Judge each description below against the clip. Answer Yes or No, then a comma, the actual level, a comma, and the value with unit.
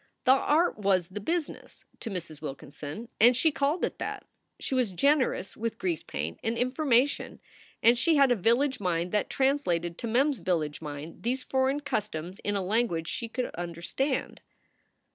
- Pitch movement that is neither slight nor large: No, wide, 7.2 semitones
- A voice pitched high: Yes, high, 230 Hz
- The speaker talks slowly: No, average, 170 wpm